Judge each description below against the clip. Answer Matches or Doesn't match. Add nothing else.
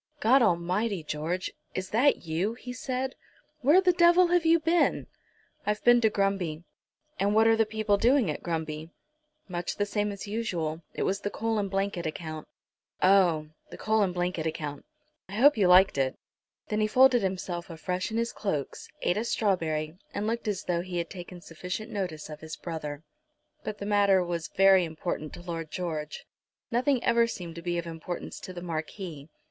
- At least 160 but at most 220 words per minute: Matches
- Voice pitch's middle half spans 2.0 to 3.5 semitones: Doesn't match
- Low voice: Doesn't match